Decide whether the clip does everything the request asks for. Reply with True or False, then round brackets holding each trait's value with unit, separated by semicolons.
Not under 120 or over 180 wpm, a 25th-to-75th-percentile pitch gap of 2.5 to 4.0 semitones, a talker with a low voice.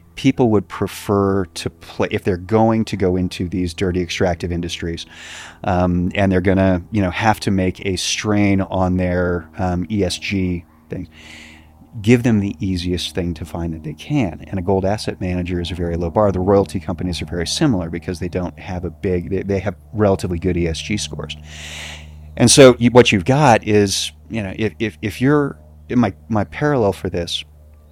False (195 wpm; 3.3 semitones; 90 Hz)